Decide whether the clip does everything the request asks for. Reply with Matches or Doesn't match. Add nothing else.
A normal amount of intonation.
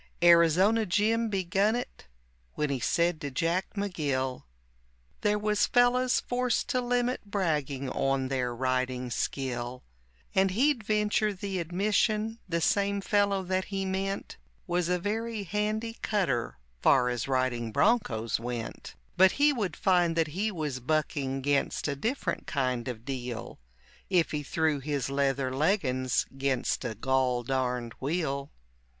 Doesn't match